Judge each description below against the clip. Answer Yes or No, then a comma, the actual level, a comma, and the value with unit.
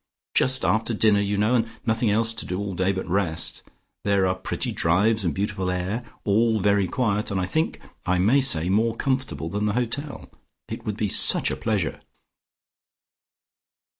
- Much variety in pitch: No, average, 3.3 semitones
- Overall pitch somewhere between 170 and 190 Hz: No, low, 105 Hz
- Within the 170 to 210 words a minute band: Yes, average, 175 wpm